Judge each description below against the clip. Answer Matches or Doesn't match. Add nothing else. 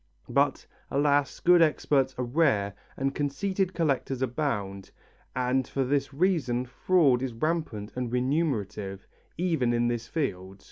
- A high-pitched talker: Doesn't match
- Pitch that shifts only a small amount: Doesn't match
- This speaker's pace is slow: Matches